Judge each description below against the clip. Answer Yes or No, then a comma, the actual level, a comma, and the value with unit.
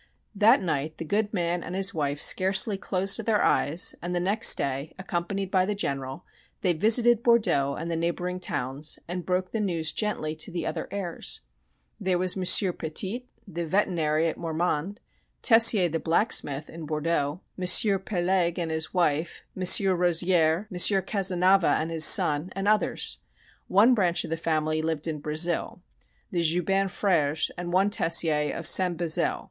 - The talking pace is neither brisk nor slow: Yes, average, 165 wpm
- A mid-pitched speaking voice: Yes, medium, 175 Hz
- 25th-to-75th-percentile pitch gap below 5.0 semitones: Yes, average, 3.4 semitones